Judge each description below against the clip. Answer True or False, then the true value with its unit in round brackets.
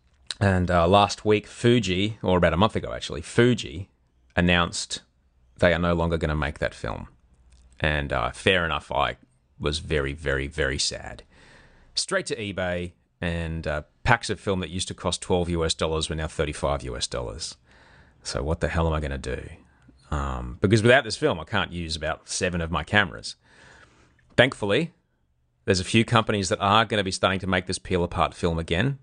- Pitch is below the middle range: True (85 Hz)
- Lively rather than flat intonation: True (5.7 semitones)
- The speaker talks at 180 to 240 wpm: True (190 wpm)